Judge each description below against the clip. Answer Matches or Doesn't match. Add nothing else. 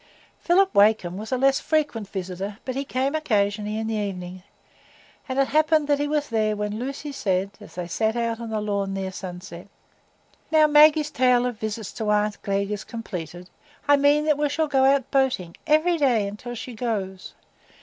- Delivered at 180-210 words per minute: Matches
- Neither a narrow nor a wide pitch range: Doesn't match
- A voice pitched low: Doesn't match